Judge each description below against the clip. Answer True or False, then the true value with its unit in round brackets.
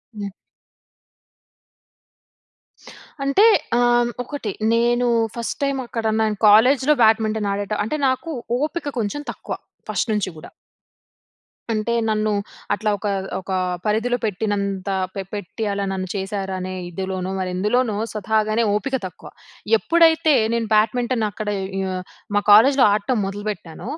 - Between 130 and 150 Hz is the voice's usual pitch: False (215 Hz)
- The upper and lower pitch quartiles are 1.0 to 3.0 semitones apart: False (3.4 semitones)